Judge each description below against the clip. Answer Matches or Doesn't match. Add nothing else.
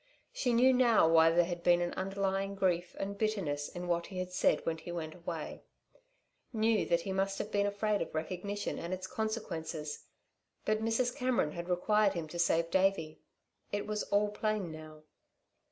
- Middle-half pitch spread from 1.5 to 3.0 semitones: Doesn't match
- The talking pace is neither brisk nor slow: Matches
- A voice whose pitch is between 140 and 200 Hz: Matches